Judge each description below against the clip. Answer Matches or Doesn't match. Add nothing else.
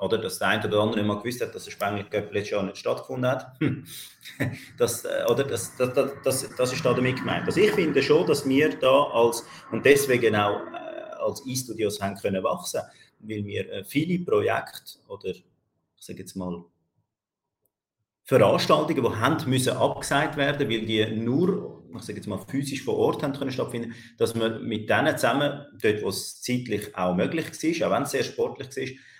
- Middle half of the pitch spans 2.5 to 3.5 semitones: Doesn't match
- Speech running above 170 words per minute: Matches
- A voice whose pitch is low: Matches